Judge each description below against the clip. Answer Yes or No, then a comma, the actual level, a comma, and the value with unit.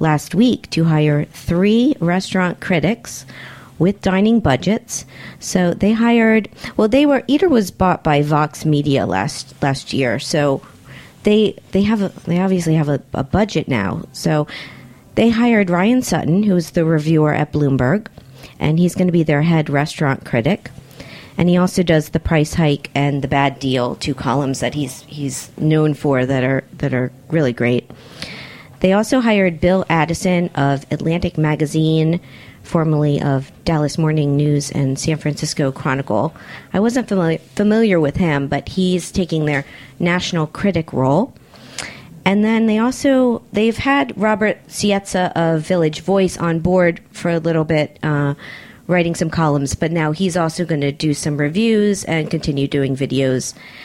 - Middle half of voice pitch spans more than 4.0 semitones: Yes, average, 4.7 semitones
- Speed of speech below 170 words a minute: Yes, average, 160 wpm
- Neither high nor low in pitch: Yes, medium, 160 Hz